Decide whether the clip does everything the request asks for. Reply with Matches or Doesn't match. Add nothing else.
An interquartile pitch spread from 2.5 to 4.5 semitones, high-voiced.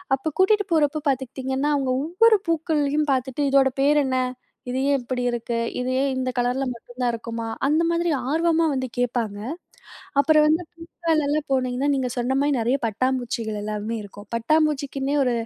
Matches